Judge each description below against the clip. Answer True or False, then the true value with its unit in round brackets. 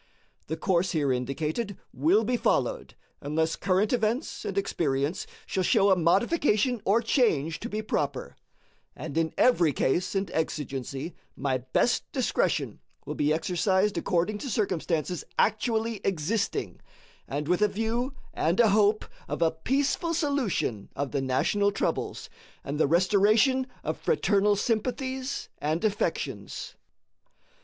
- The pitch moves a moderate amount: False (5.9 semitones)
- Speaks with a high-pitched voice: True (195 Hz)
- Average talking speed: False (130 wpm)